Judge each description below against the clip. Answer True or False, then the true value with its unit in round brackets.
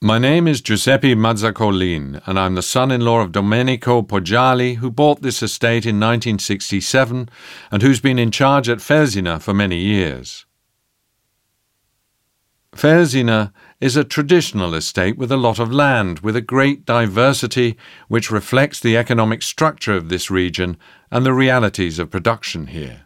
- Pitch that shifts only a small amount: False (4.3 semitones)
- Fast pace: False (145 wpm)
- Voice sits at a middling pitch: False (115 Hz)